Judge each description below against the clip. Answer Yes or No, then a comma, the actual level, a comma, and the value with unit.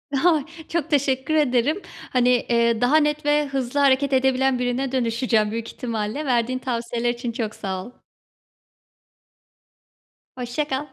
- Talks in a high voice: Yes, very high, 255 Hz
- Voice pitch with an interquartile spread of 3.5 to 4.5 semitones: No, average, 3.1 semitones